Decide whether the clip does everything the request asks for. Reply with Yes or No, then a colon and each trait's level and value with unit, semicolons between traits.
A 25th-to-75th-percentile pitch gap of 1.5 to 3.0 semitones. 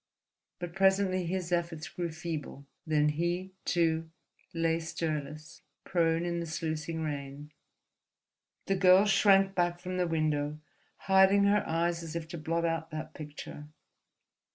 Yes: narrow, 2.6 semitones